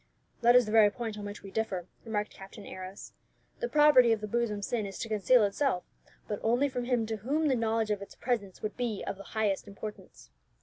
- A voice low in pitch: No, high, 220 Hz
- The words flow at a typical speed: No, fast, 220 wpm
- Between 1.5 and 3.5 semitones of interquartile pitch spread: Yes, average, 2.9 semitones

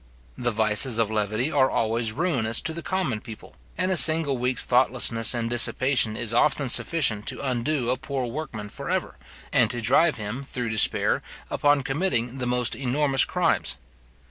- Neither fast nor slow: Yes, average, 170 wpm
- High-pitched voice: No, low, 125 Hz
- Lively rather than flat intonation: No, average, 3.7 semitones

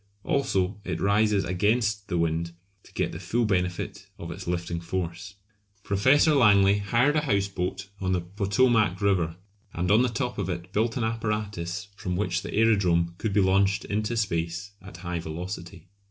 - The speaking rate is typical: Yes, average, 170 wpm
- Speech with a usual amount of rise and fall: Yes, average, 3.2 semitones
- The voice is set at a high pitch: No, low, 100 Hz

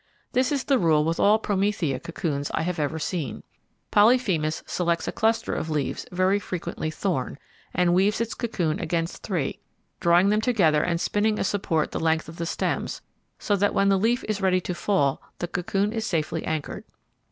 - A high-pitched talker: No, medium, 180 Hz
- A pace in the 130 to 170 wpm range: No, average, 185 wpm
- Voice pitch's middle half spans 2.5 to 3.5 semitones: No, average, 4.3 semitones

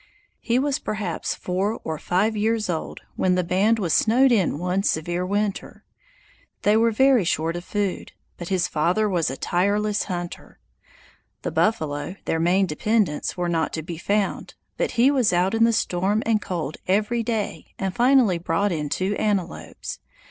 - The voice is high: Yes, high, 195 Hz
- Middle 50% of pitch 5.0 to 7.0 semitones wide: No, average, 3.8 semitones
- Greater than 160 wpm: Yes, average, 170 wpm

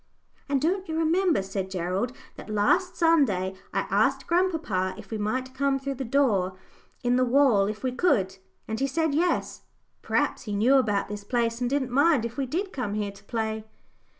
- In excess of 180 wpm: Yes, average, 190 wpm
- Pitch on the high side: Yes, high, 245 Hz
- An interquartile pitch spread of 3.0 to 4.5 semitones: No, wide, 5.5 semitones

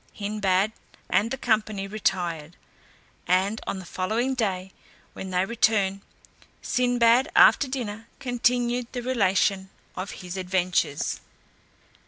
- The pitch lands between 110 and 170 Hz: No, high, 205 Hz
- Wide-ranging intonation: No, average, 4.2 semitones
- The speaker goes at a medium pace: No, slow, 110 wpm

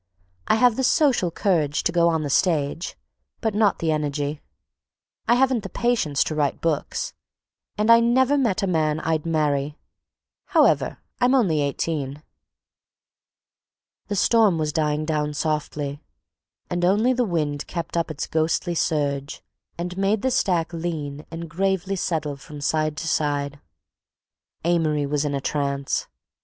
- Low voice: No, medium, 160 Hz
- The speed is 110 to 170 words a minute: Yes, average, 150 wpm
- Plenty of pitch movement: No, average, 4.7 semitones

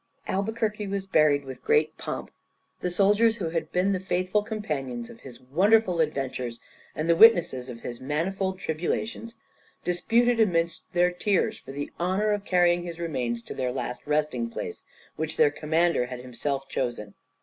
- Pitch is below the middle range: No, medium, 175 Hz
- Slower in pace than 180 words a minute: Yes, average, 160 wpm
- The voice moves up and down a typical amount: No, wide, 6.7 semitones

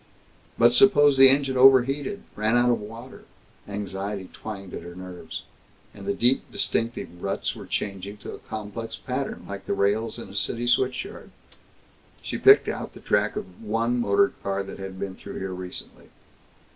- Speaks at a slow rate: No, average, 170 wpm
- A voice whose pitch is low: Yes, low, 105 Hz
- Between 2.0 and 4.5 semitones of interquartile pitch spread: Yes, average, 3.9 semitones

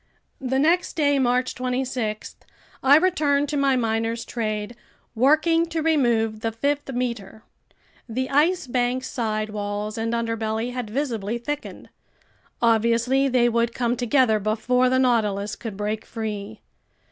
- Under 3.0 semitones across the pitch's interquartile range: No, average, 3.4 semitones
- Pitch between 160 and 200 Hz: No, high, 240 Hz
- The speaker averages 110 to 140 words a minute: Yes, slow, 135 wpm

